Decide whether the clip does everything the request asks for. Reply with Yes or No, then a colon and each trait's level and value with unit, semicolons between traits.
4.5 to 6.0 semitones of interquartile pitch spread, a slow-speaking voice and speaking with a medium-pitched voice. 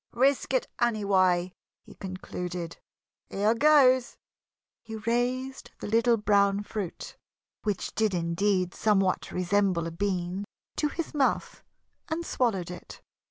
No: average, 4.8 semitones; slow, 115 wpm; high, 205 Hz